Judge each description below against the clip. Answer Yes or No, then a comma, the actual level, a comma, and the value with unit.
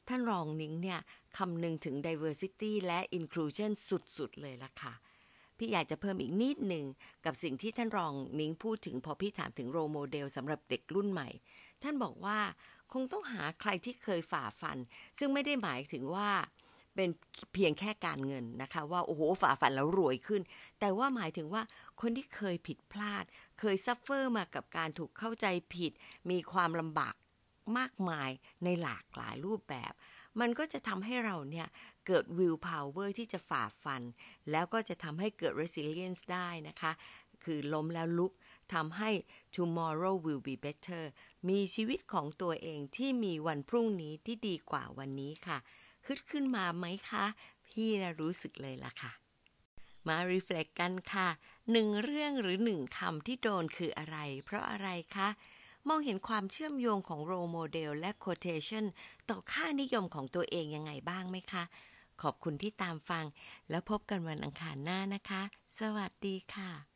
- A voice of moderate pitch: Yes, medium, 180 Hz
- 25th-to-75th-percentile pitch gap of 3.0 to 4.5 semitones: No, average, 5.1 semitones